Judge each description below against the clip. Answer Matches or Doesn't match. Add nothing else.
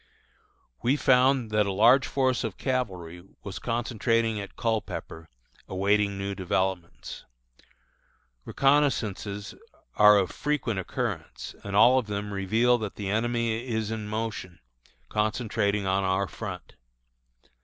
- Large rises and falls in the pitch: Doesn't match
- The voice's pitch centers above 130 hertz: Doesn't match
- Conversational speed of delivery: Doesn't match